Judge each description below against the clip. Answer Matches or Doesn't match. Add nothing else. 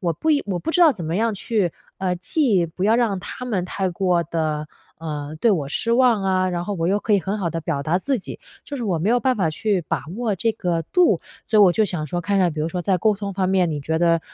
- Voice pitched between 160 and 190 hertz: Matches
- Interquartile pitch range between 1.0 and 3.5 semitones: Doesn't match